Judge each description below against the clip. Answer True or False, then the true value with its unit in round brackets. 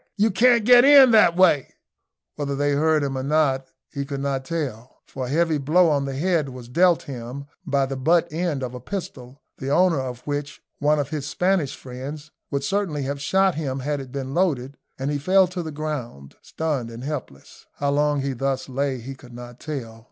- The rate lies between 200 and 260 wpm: True (205 wpm)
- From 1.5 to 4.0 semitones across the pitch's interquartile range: True (3.4 semitones)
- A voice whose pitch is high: False (140 Hz)